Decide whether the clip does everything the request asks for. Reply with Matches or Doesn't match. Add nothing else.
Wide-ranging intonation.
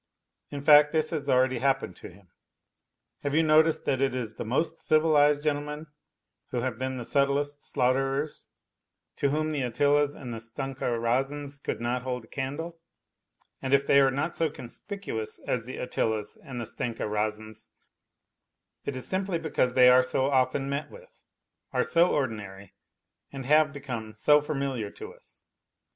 Doesn't match